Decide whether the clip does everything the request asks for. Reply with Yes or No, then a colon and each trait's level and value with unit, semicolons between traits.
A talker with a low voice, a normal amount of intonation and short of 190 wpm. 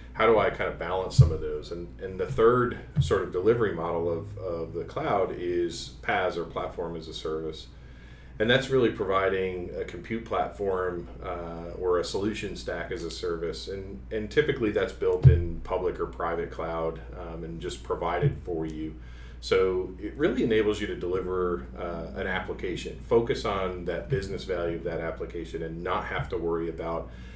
Yes: very low, 90 Hz; average, 3.7 semitones; average, 180 wpm